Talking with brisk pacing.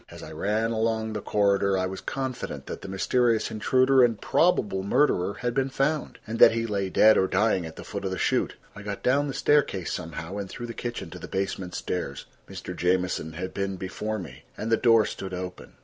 Yes: fast, 215 wpm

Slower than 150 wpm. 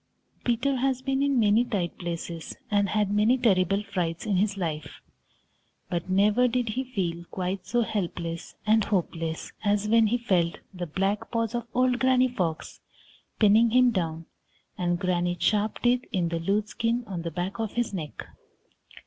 No: average, 165 wpm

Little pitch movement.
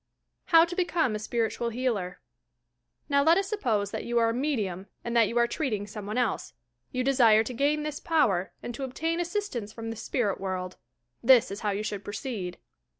No: wide, 5.4 semitones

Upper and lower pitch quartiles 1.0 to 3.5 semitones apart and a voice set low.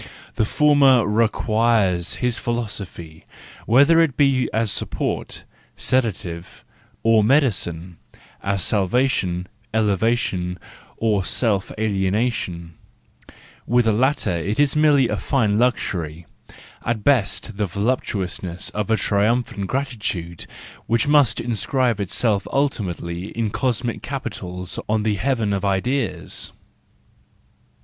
No: average, 4.7 semitones; low, 110 Hz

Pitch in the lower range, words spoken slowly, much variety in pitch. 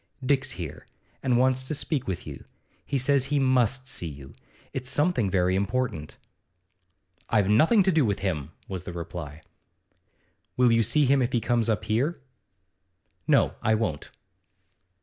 No: low, 120 Hz; average, 155 wpm; wide, 6.1 semitones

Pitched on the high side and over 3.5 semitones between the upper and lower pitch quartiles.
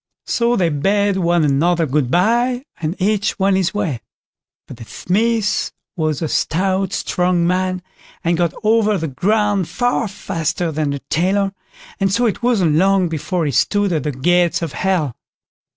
No: medium, 180 Hz; average, 4.0 semitones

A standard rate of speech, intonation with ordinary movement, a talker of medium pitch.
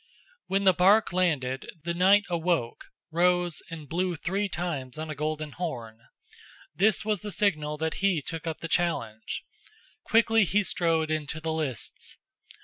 Yes: average, 150 wpm; average, 3.3 semitones; medium, 165 Hz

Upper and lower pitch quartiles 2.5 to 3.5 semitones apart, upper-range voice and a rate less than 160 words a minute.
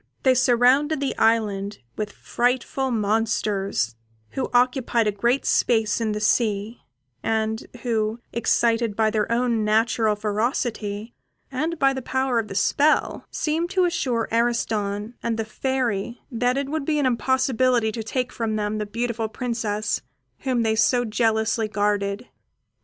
Yes: average, 2.9 semitones; high, 230 Hz; average, 145 wpm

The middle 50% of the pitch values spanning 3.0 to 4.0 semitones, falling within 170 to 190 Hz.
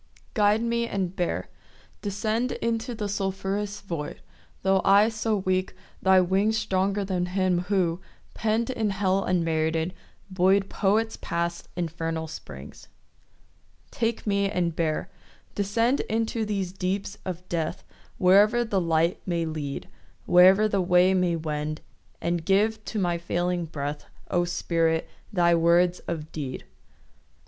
Yes: average, 3.3 semitones; medium, 185 Hz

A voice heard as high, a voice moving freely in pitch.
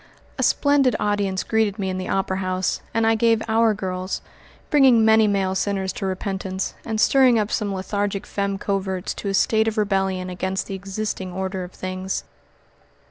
No: high, 195 Hz; narrow, 2.6 semitones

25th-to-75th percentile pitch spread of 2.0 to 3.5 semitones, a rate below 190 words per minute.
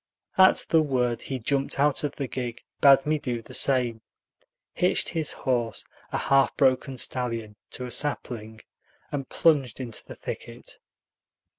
Yes: average, 2.9 semitones; average, 150 wpm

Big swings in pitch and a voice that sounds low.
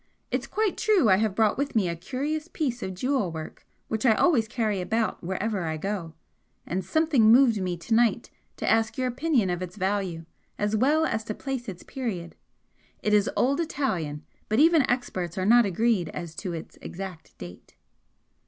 No: wide, 5.9 semitones; high, 215 Hz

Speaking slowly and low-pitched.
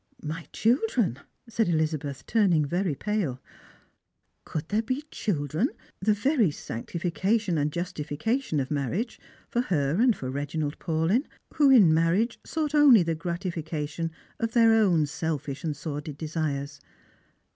No: slow, 130 wpm; medium, 165 Hz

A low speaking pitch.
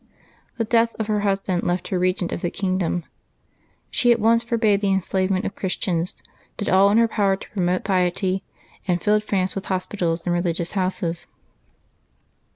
No: high, 190 Hz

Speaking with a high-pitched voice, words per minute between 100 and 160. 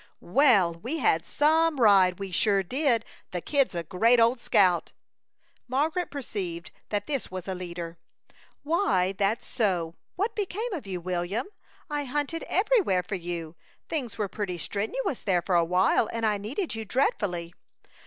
Yes: high, 210 Hz; average, 155 wpm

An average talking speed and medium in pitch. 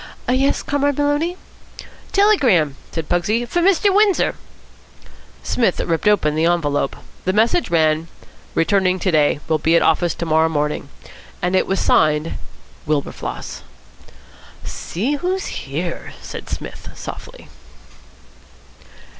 No: slow, 120 wpm; medium, 180 Hz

